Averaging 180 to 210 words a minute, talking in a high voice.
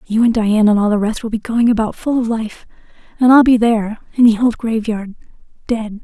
Yes: average, 200 wpm; high, 225 Hz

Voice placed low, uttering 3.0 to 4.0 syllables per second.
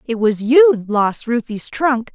No: high, 240 Hz; 3.5 syllables/s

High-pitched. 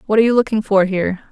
Yes: high, 205 Hz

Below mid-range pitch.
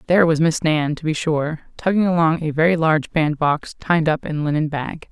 No: medium, 160 Hz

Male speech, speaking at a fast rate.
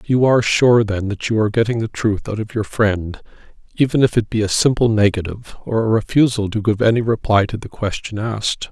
Yes: male; fast, 220 wpm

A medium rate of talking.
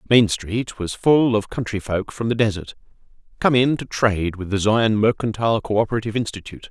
Yes: average, 180 wpm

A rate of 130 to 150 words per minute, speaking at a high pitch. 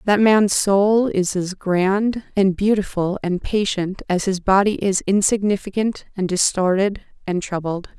Yes: average, 145 wpm; high, 195 Hz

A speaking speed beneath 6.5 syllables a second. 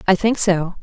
Yes: 4.8 syllables/s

